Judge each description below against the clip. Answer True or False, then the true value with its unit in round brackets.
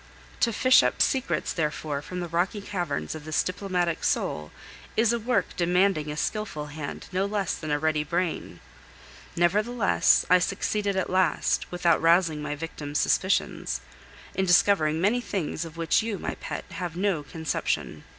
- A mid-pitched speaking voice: True (175 Hz)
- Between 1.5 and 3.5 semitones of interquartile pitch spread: False (4.2 semitones)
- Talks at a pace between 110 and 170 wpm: True (160 wpm)